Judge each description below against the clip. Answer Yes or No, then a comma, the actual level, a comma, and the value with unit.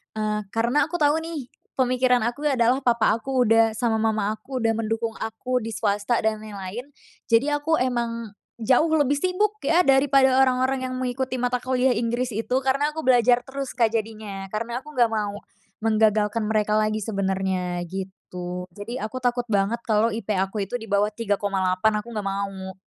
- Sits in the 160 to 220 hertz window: No, high, 230 Hz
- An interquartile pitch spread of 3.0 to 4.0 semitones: Yes, average, 3.3 semitones